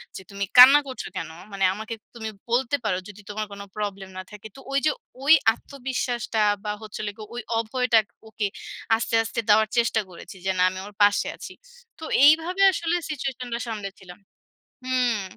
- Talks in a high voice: Yes, high, 225 Hz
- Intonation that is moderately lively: Yes, average, 3.7 semitones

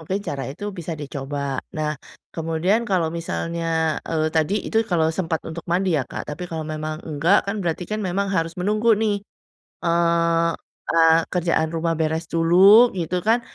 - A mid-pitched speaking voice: Yes, medium, 165 Hz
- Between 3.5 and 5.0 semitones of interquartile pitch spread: No, average, 2.8 semitones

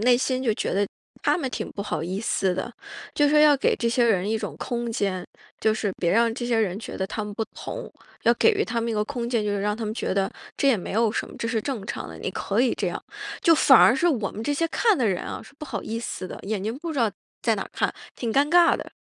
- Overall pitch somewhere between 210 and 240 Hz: Yes, high, 230 Hz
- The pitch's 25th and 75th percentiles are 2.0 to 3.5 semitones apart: No, average, 4.2 semitones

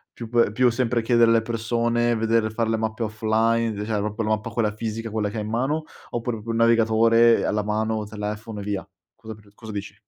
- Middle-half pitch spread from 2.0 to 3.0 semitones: No, narrow, 1.4 semitones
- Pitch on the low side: Yes, low, 110 Hz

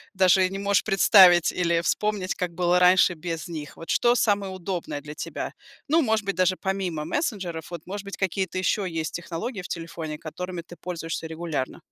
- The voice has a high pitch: No, medium, 180 Hz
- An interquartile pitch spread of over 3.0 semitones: No, average, 2.7 semitones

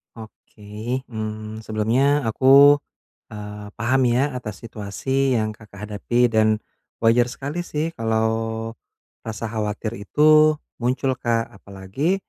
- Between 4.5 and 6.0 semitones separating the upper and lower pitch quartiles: No, average, 3.6 semitones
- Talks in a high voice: No, low, 115 Hz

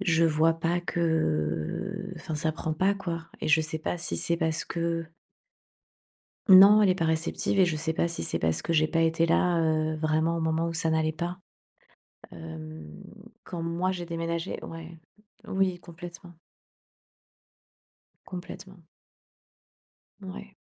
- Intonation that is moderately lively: No, narrow, 1.8 semitones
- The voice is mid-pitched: Yes, medium, 165 Hz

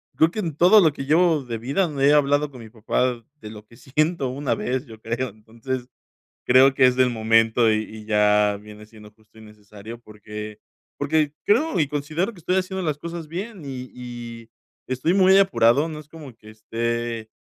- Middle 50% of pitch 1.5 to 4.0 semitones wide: No, wide, 5.6 semitones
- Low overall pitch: Yes, low, 125 Hz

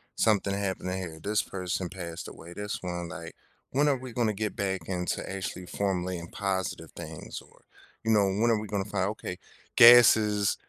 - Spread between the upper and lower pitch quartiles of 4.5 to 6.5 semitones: No, average, 2.7 semitones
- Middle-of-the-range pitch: No, very low, 95 Hz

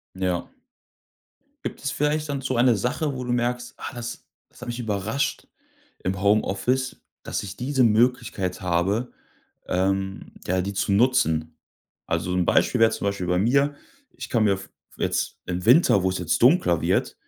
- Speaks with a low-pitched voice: Yes, low, 110 Hz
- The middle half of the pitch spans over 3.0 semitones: Yes, average, 5.0 semitones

